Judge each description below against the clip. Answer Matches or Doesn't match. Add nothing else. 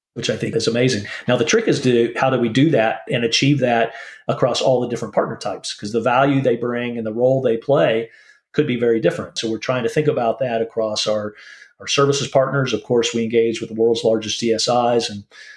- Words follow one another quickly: Matches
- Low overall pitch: Matches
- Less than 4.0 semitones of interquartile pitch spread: Matches